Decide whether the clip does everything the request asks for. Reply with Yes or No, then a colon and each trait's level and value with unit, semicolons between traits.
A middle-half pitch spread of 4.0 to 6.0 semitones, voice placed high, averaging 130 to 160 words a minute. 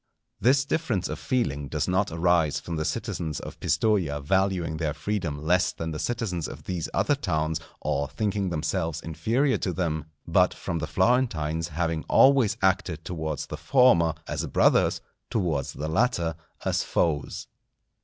No: average, 4.7 semitones; very low, 85 Hz; average, 155 wpm